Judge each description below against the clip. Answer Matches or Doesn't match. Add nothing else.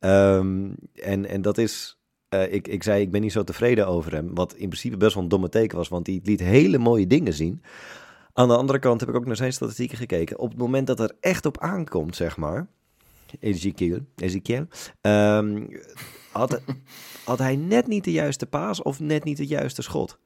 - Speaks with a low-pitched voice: Matches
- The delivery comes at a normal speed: Doesn't match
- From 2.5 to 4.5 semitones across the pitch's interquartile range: Doesn't match